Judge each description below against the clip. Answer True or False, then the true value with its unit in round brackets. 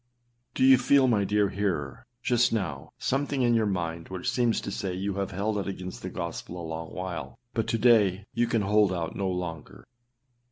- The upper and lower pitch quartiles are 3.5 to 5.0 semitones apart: True (4.3 semitones)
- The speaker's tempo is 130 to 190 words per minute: False (200 wpm)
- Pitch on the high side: False (100 Hz)